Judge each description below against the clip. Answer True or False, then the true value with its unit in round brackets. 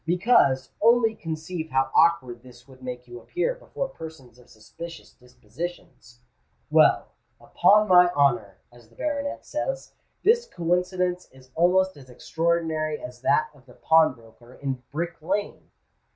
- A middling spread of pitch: False (6.1 semitones)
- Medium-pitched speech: True (160 Hz)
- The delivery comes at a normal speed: False (130 wpm)